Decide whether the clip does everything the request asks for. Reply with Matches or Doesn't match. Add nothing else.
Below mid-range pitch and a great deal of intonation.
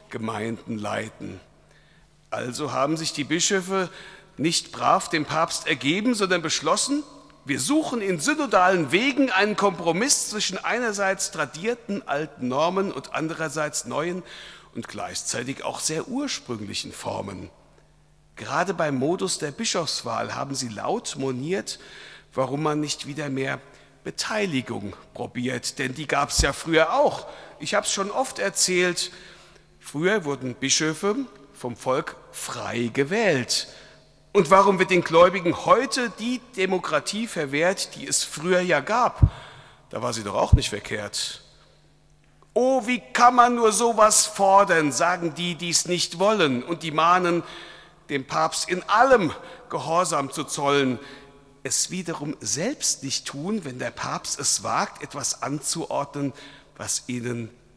Doesn't match